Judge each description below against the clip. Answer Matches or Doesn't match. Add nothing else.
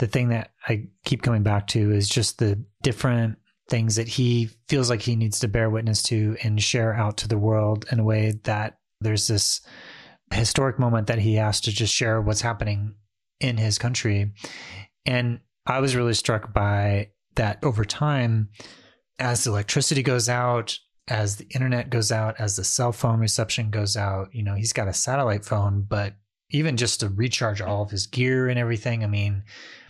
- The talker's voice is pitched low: Matches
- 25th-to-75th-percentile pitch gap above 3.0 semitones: Doesn't match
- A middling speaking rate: Matches